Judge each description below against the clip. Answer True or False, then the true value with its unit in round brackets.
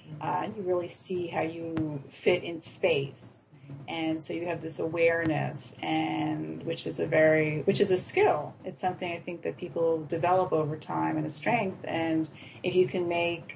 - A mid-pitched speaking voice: True (165 Hz)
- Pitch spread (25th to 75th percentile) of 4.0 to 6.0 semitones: False (2.4 semitones)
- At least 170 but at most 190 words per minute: True (180 wpm)